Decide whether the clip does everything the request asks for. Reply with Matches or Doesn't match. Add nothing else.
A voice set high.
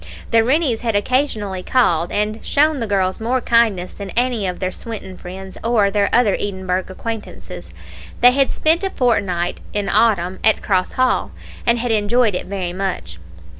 Matches